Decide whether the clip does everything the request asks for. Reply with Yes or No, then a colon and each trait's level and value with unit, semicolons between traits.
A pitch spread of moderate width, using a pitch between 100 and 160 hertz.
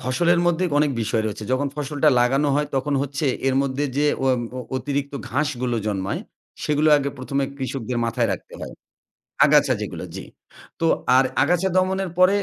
Yes: average, 3.0 semitones; medium, 140 Hz